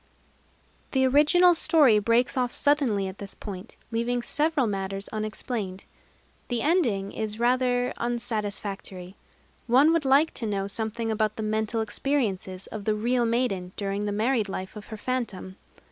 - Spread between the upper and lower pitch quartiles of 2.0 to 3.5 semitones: No, average, 3.9 semitones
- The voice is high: Yes, high, 225 Hz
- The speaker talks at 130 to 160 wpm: Yes, average, 150 wpm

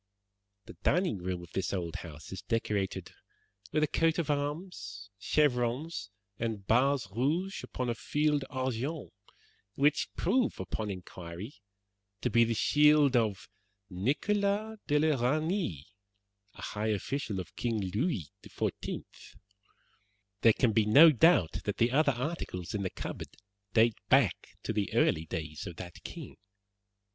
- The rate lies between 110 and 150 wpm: Yes, average, 140 wpm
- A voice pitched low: Yes, low, 120 Hz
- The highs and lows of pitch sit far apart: Yes, wide, 7.0 semitones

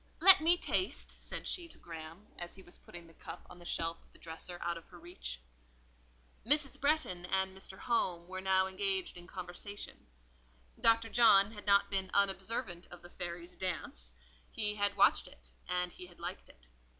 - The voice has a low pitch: No, medium, 185 Hz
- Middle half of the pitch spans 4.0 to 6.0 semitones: No, average, 2.7 semitones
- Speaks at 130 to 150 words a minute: No, average, 185 wpm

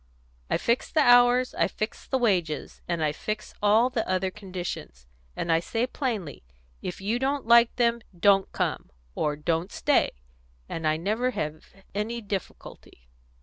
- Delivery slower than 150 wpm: No, average, 160 wpm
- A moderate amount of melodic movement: No, wide, 6.0 semitones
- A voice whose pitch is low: No, high, 205 Hz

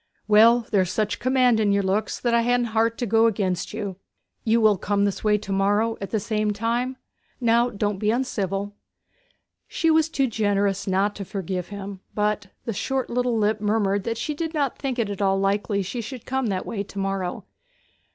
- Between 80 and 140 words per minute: No, average, 200 wpm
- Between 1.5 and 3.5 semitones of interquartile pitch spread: Yes, average, 2.8 semitones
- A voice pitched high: Yes, high, 210 Hz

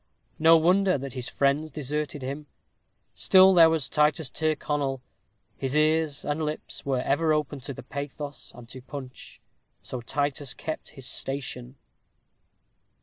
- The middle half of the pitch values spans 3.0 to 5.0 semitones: No, narrow, 2.6 semitones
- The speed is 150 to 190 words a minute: No, slow, 135 wpm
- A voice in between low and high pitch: Yes, medium, 145 Hz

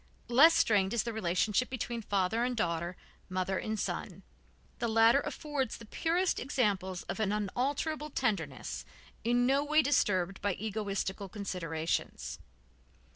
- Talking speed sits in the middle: No, slow, 130 wpm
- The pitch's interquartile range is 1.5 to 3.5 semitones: No, average, 5.1 semitones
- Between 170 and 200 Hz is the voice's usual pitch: No, high, 220 Hz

